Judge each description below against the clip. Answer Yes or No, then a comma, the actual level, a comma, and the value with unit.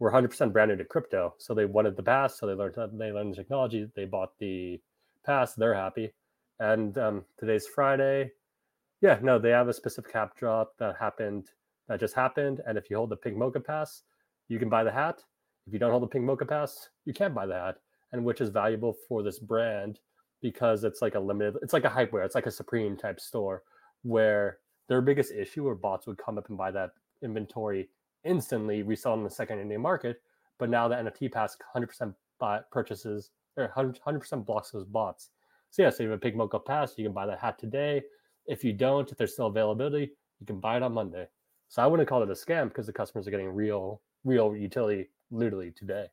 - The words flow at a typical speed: No, fast, 220 wpm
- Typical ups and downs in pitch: Yes, average, 3.5 semitones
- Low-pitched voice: Yes, low, 110 Hz